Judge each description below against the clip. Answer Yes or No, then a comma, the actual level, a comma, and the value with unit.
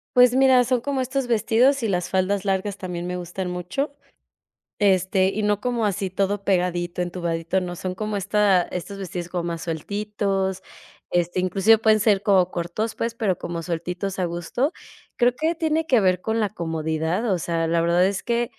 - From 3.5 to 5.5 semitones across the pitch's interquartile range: Yes, average, 3.8 semitones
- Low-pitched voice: No, high, 190 Hz